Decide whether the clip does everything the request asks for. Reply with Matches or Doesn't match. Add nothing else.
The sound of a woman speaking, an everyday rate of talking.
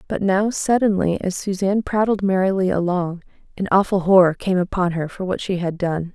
Matches